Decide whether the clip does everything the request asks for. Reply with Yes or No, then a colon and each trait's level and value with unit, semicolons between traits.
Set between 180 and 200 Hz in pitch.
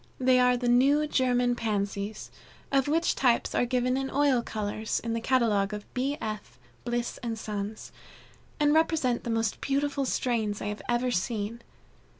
No: high, 240 Hz